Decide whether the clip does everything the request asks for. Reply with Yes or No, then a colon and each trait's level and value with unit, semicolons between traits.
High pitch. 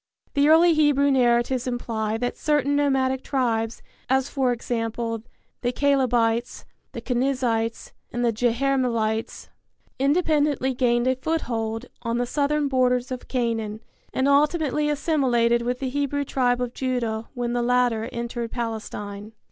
Yes: very high, 250 Hz